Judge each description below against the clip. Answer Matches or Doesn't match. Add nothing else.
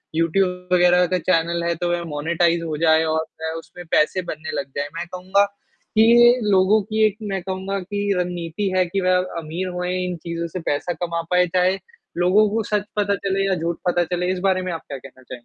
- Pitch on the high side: Doesn't match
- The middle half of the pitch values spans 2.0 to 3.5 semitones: Matches